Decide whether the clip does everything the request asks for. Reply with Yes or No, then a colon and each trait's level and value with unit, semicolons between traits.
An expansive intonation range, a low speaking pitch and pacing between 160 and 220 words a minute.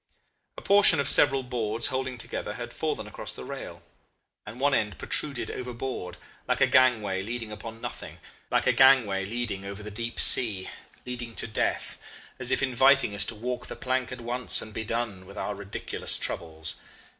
No: average, 3.6 semitones; low, 120 Hz; average, 180 wpm